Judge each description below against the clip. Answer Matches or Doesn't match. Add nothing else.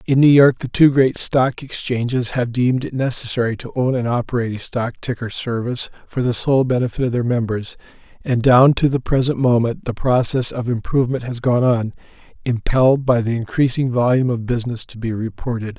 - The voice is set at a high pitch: Doesn't match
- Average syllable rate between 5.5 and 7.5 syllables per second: Matches